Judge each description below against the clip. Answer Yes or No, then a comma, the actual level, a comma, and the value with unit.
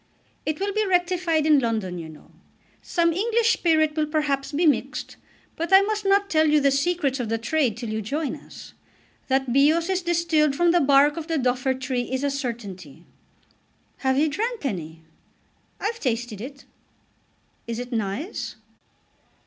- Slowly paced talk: No, average, 165 wpm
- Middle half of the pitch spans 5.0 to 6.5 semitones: Yes, wide, 5.5 semitones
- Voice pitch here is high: Yes, very high, 290 Hz